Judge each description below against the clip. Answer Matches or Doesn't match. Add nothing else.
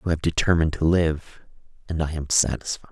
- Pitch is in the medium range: Doesn't match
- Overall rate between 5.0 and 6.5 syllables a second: Matches